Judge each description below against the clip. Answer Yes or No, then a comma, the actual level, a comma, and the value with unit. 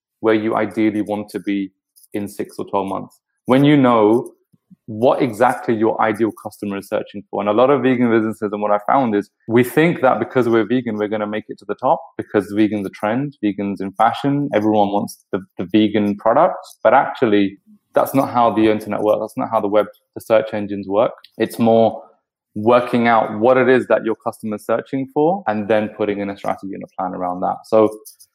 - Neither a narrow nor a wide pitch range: No, narrow, 2.1 semitones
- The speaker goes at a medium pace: No, fast, 220 wpm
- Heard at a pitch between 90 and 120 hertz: Yes, low, 110 Hz